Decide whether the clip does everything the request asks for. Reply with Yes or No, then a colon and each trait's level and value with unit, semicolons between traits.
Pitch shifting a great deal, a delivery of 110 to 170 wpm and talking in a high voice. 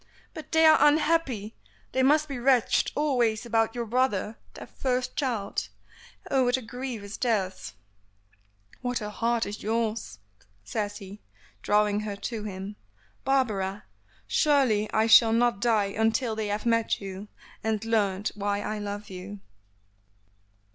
No: average, 3.3 semitones; average, 140 wpm; high, 220 Hz